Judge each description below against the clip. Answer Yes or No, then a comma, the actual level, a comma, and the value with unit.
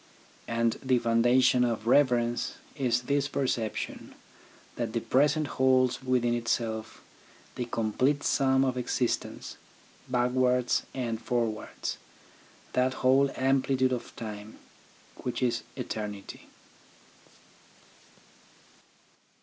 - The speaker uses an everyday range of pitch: No, narrow, 2.0 semitones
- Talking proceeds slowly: Yes, slow, 95 wpm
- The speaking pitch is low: Yes, low, 125 Hz